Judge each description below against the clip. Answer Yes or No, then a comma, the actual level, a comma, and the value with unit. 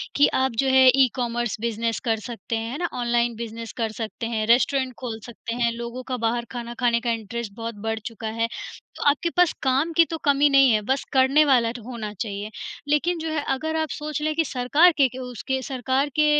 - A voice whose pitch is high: Yes, high, 245 Hz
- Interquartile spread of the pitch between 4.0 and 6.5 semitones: No, average, 3.1 semitones